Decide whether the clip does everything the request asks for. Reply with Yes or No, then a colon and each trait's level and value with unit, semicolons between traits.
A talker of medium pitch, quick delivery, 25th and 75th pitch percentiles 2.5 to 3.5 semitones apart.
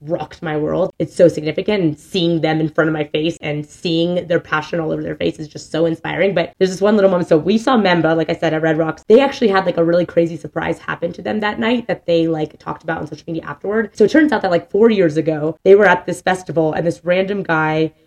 Yes: medium, 170 Hz; fast, 270 wpm; average, 2.9 semitones